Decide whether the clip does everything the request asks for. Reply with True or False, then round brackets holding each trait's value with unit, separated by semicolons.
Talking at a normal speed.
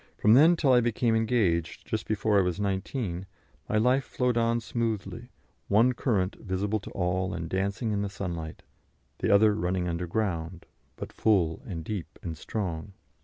True (165 wpm)